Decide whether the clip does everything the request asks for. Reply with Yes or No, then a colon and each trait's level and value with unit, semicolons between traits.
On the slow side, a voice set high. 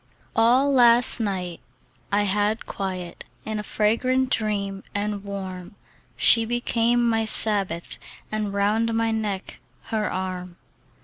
Yes: slow, 120 wpm; high, 210 Hz